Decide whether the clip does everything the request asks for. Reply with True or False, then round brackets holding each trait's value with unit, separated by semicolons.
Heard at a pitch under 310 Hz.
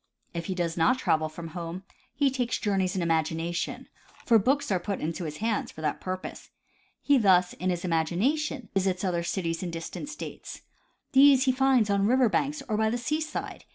True (190 Hz)